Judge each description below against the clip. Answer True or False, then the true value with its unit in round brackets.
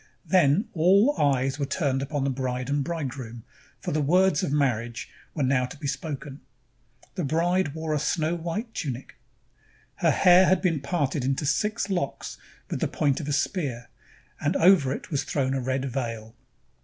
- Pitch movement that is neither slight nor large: True (4.2 semitones)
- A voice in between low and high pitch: True (145 Hz)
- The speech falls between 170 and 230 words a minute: True (175 wpm)